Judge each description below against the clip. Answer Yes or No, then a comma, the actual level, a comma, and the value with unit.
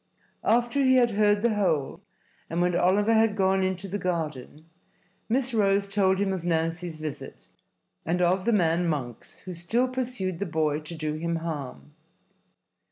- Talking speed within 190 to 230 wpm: No, average, 165 wpm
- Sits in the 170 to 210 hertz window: Yes, medium, 185 Hz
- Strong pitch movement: No, average, 4.2 semitones